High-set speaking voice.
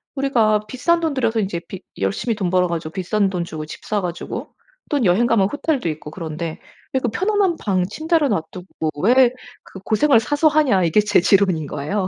Yes: high, 205 Hz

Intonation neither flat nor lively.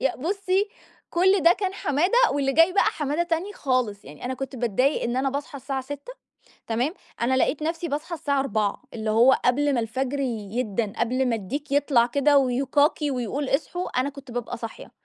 Yes: average, 3.7 semitones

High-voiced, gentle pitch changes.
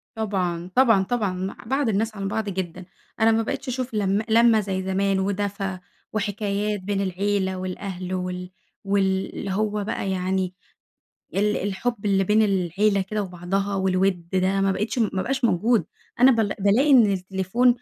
Yes: high, 200 Hz; narrow, 2.3 semitones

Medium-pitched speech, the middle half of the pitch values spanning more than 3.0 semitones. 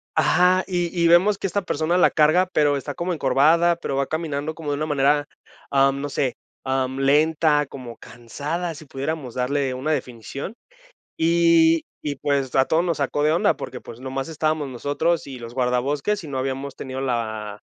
Yes: medium, 145 Hz; average, 3.5 semitones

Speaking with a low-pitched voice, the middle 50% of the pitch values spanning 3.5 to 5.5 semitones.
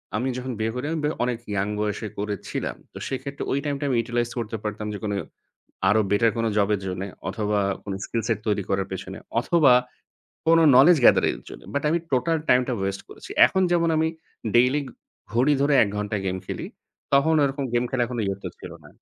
Yes: low, 120 Hz; average, 5.0 semitones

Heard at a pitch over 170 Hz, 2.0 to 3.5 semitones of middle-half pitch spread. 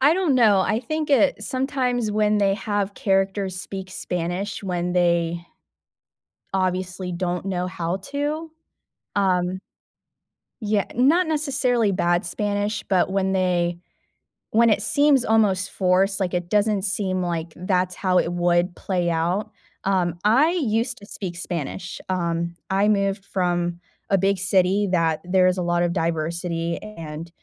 Yes: high, 190 Hz; average, 3.1 semitones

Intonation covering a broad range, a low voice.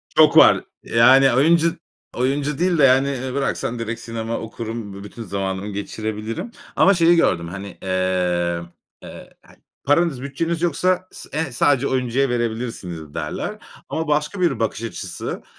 Yes: wide, 6.0 semitones; low, 120 Hz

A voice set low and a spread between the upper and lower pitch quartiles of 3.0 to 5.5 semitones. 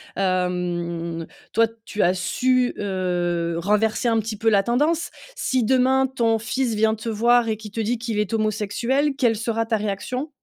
No: high, 220 Hz; average, 3.6 semitones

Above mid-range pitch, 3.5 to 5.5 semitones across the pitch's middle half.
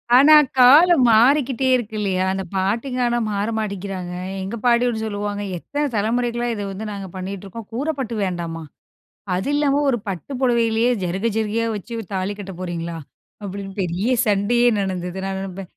Yes: high, 210 Hz; average, 4.0 semitones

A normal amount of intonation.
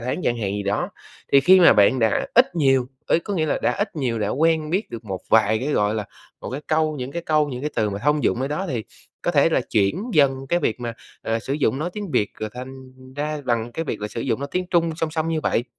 No: wide, 5.7 semitones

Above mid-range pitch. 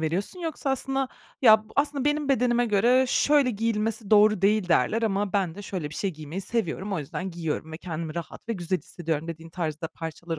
Yes: high, 200 Hz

